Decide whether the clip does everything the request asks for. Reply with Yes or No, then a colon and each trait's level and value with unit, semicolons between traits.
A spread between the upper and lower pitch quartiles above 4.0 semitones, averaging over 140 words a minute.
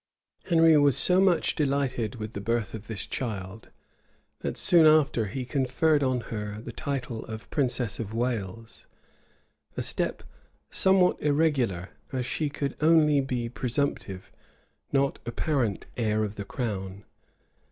No: average, 4.9 semitones; slow, 135 wpm